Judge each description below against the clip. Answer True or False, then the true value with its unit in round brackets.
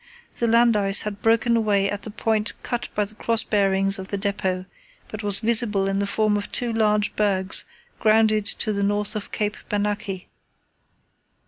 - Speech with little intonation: True (1.6 semitones)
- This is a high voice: True (210 Hz)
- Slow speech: False (180 wpm)